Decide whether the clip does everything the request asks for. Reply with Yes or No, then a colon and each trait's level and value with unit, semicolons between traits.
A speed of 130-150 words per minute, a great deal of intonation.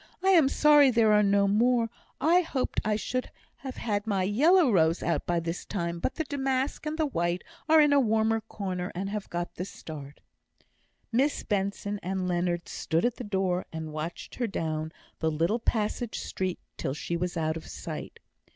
No: average, 190 wpm; wide, 6.5 semitones